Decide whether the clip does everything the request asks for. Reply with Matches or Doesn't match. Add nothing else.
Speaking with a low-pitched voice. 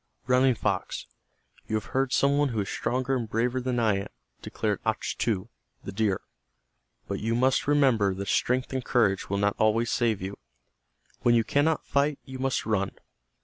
Matches